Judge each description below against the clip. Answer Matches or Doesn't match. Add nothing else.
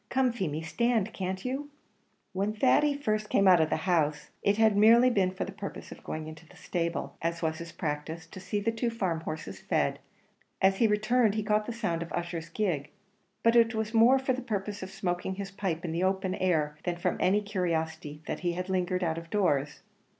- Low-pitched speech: Doesn't match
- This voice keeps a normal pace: Doesn't match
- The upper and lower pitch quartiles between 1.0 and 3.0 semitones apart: Doesn't match